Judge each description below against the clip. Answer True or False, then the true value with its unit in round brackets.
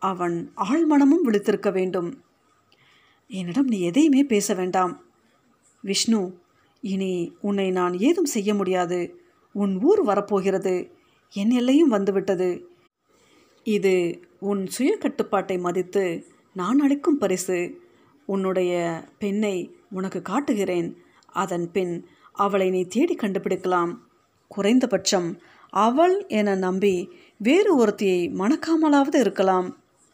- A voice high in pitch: True (200 Hz)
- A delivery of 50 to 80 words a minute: False (95 wpm)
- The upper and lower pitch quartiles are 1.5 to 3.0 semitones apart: False (5.0 semitones)